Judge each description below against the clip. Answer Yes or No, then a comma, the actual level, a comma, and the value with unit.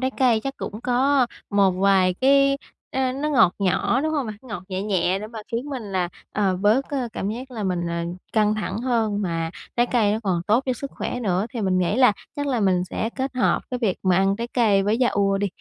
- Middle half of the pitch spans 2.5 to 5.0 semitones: Yes, average, 4.7 semitones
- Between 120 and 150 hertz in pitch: No, high, 215 Hz